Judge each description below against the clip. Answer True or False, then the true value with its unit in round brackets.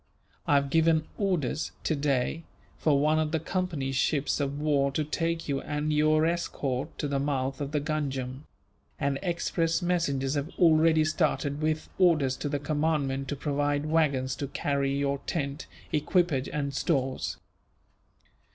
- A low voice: False (145 Hz)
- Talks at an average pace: True (150 wpm)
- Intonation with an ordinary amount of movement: False (2.3 semitones)